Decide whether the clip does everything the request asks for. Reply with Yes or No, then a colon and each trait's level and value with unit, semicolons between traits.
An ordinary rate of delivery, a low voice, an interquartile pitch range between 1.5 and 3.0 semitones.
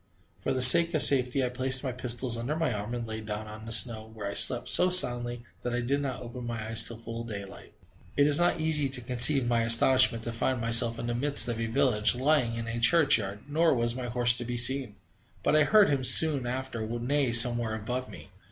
No: fast, 235 wpm; low, 120 Hz; narrow, 2.5 semitones